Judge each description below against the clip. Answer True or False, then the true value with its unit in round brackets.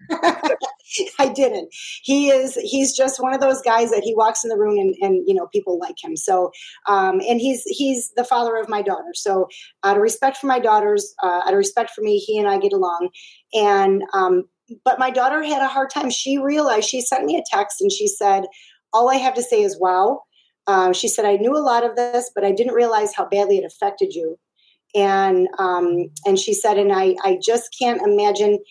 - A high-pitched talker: True (255 Hz)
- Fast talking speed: True (220 wpm)